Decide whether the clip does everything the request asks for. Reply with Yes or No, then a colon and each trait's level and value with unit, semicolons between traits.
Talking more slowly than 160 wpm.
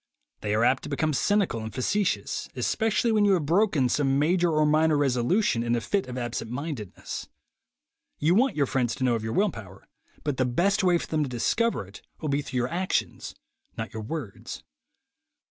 No: average, 200 wpm